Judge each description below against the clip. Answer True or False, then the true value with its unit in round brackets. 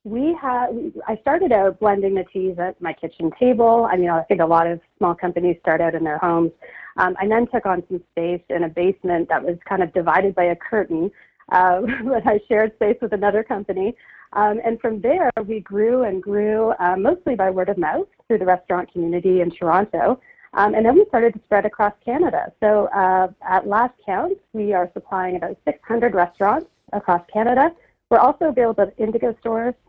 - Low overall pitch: False (200 Hz)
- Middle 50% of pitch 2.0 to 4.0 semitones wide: False (4.5 semitones)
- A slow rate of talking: False (200 wpm)